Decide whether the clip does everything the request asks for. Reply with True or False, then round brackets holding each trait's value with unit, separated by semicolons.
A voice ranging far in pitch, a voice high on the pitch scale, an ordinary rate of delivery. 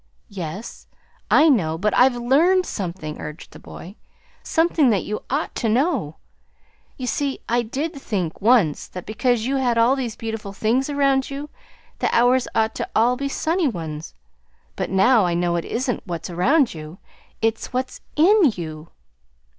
True (6.7 semitones; 230 Hz; 165 wpm)